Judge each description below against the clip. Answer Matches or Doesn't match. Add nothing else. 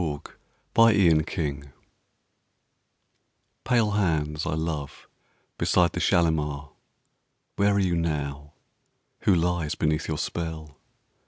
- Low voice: Matches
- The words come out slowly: Matches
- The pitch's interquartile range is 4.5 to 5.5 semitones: Doesn't match